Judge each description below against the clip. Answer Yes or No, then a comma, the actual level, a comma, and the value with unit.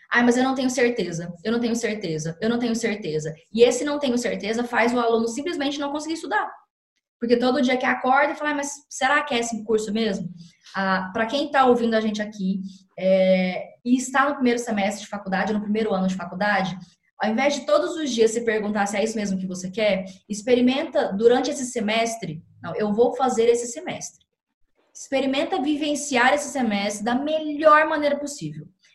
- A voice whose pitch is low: No, high, 230 Hz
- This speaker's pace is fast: Yes, fast, 195 wpm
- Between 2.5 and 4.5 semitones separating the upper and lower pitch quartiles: No, average, 5.1 semitones